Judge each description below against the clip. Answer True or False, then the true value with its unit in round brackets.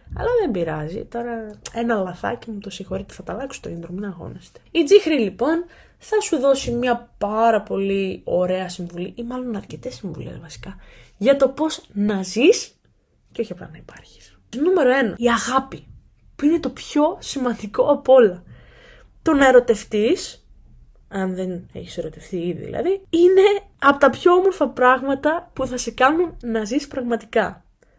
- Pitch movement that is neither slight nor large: False (6.4 semitones)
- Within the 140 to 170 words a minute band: True (160 wpm)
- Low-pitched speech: False (240 Hz)